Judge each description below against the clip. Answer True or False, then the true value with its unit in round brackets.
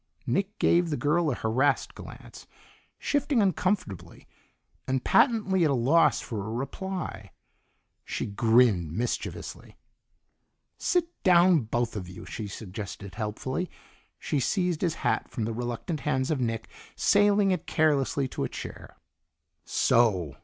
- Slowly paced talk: True (130 wpm)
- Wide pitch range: True (8.1 semitones)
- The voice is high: False (135 Hz)